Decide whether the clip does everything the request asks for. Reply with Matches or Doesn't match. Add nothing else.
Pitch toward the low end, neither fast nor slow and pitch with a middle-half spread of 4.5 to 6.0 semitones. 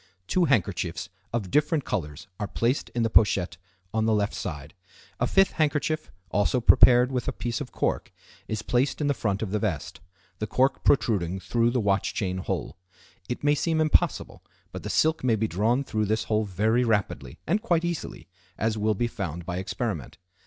Matches